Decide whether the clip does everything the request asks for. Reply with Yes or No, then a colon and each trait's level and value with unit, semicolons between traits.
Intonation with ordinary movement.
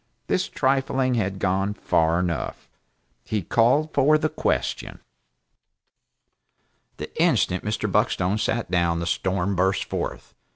No: wide, 5.7 semitones